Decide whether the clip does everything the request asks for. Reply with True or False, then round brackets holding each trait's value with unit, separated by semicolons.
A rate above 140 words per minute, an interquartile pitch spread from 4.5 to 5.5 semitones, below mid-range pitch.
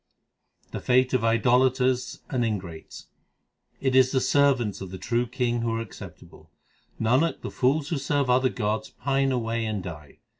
False (160 wpm; 2.7 semitones; 125 Hz)